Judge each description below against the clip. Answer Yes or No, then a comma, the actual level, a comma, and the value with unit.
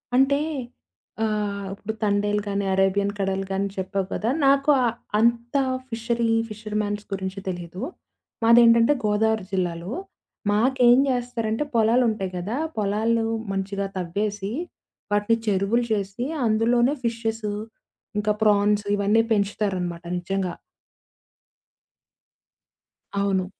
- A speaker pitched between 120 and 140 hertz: No, high, 210 Hz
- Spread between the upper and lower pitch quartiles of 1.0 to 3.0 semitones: Yes, narrow, 2.6 semitones